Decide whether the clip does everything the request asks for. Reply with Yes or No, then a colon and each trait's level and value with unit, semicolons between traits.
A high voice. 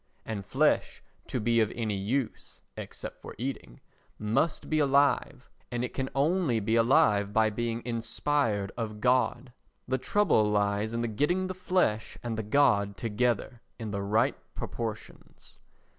No: low, 115 Hz